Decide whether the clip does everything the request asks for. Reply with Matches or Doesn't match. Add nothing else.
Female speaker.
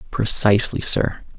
Doesn't match